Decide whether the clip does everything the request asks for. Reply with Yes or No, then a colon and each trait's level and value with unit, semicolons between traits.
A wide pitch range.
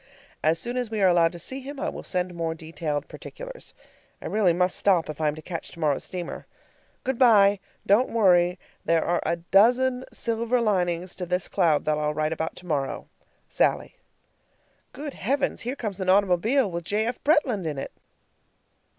Yes: wide, 5.7 semitones